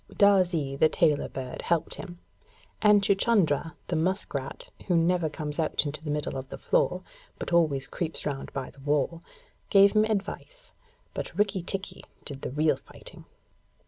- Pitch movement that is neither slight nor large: Yes, average, 5.0 semitones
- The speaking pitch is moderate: Yes, medium, 165 Hz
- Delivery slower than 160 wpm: No, average, 165 wpm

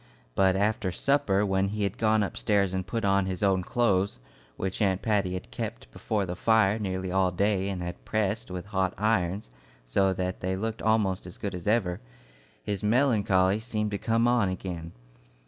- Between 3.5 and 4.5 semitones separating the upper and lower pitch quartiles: No, narrow, 2.5 semitones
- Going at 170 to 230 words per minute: Yes, average, 180 wpm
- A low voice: Yes, low, 100 Hz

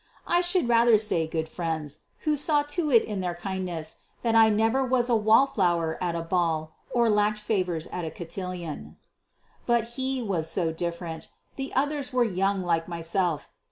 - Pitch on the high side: Yes, high, 195 Hz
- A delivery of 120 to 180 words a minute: Yes, average, 175 wpm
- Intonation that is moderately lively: No, wide, 6.0 semitones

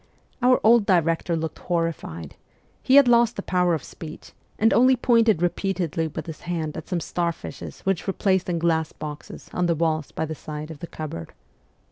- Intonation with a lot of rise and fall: No, average, 3.4 semitones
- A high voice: No, medium, 170 Hz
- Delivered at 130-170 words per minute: No, average, 190 wpm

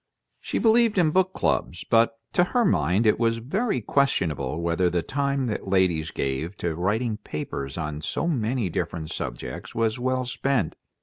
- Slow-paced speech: No, average, 165 wpm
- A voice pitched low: Yes, low, 110 Hz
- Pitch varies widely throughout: Yes, wide, 8.3 semitones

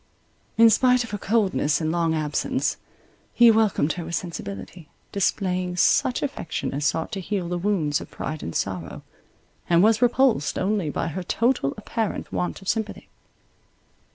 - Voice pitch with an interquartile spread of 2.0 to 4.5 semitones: No, wide, 5.4 semitones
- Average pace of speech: Yes, average, 155 wpm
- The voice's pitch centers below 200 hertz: Yes, medium, 185 Hz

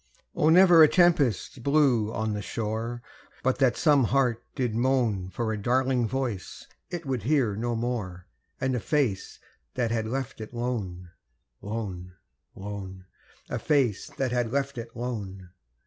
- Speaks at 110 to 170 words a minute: Yes, average, 150 wpm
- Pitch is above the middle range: No, low, 120 Hz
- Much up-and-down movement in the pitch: No, average, 4.0 semitones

